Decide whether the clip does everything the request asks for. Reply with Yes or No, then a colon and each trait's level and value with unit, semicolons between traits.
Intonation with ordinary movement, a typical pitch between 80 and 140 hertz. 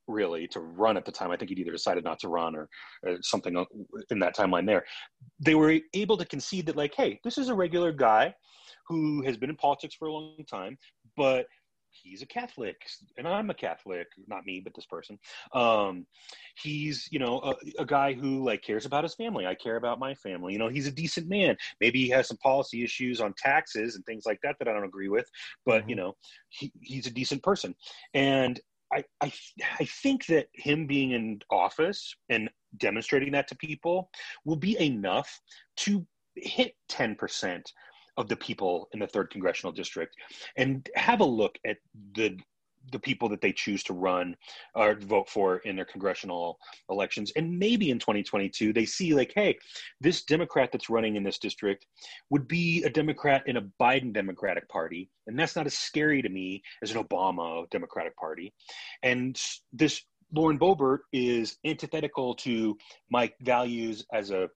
No: wide, 6.2 semitones; low, 135 Hz